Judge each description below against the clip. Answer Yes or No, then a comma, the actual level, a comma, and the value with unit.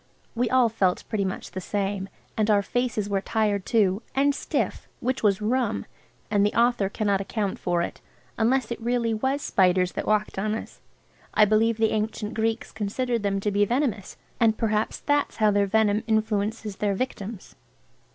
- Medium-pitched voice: No, high, 215 Hz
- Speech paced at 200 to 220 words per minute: No, average, 175 wpm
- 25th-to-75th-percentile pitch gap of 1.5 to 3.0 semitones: Yes, narrow, 2.4 semitones